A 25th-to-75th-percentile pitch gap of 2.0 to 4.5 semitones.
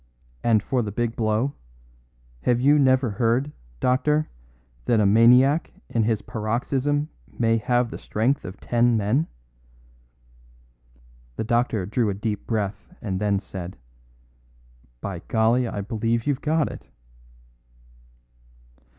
Yes: average, 3.2 semitones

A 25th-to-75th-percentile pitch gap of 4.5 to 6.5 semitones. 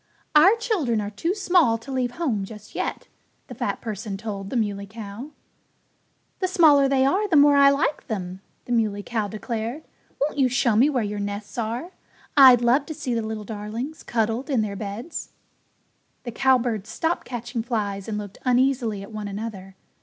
Yes: average, 4.8 semitones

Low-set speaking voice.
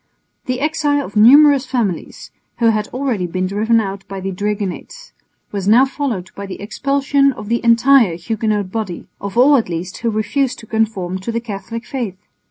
No: high, 220 Hz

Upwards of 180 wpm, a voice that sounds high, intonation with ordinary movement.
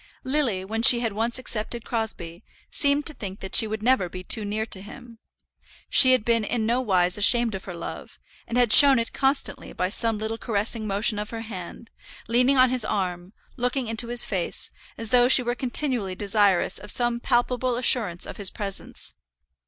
Yes: average, 190 wpm; high, 225 Hz; average, 3.4 semitones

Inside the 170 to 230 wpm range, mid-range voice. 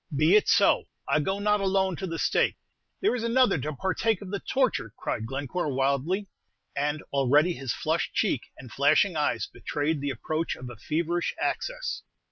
Yes: average, 175 wpm; medium, 160 Hz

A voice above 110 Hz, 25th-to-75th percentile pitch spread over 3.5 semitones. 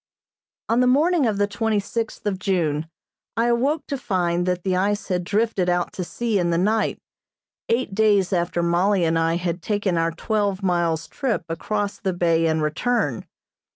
Yes: high, 190 Hz; average, 4.1 semitones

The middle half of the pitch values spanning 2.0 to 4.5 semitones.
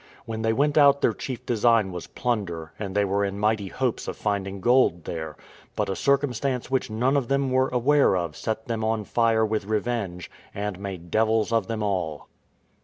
Yes: average, 3.9 semitones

